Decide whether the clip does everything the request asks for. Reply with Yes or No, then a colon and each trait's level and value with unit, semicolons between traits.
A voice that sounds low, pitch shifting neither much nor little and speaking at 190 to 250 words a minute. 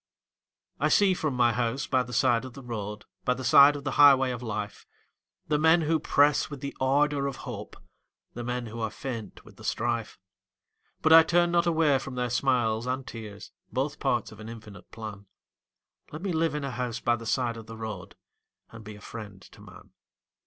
Yes: low, 125 Hz; average, 4.1 semitones; fast, 205 wpm